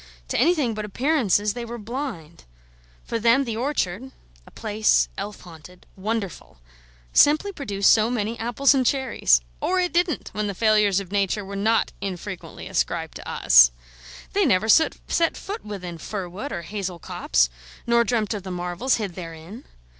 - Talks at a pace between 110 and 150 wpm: No, average, 160 wpm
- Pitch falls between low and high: No, high, 210 Hz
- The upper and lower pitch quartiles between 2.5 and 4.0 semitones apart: No, average, 4.6 semitones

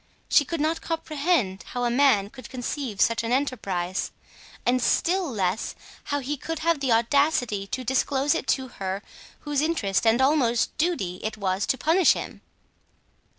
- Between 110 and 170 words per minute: Yes, average, 160 wpm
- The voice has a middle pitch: No, very high, 255 Hz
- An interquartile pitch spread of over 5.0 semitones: Yes, wide, 5.5 semitones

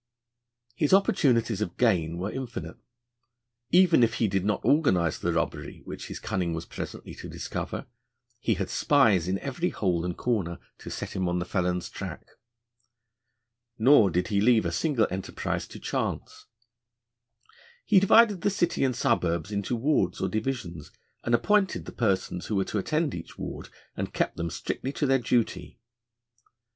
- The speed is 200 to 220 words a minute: No, average, 160 wpm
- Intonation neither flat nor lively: No, wide, 7.0 semitones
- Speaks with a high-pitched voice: No, low, 110 Hz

